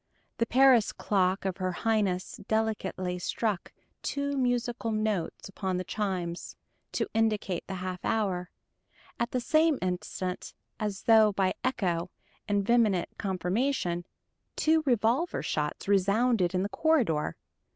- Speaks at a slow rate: Yes, slow, 125 wpm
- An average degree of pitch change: Yes, average, 4.2 semitones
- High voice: Yes, high, 205 Hz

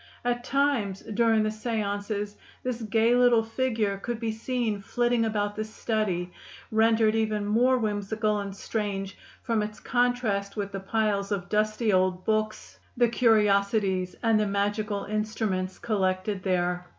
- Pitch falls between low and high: No, high, 215 Hz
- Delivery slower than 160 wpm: Yes, average, 140 wpm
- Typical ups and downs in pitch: No, narrow, 2.2 semitones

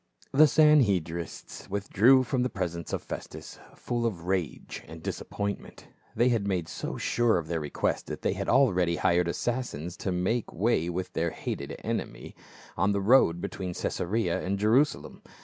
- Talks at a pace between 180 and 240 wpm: No, average, 160 wpm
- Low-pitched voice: Yes, very low, 95 Hz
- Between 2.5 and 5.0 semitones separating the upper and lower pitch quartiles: No, wide, 5.6 semitones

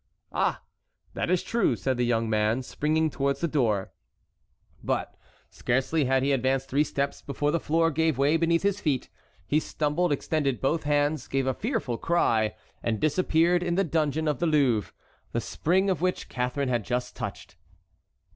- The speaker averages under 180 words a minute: Yes, average, 170 wpm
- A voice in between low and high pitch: Yes, medium, 145 Hz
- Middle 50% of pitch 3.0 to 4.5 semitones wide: Yes, average, 3.9 semitones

